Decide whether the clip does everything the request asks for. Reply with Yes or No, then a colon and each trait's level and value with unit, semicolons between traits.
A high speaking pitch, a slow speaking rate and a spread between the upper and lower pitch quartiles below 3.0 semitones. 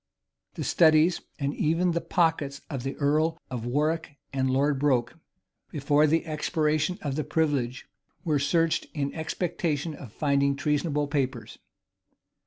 No: medium, 150 Hz; slow, 130 wpm; narrow, 2.4 semitones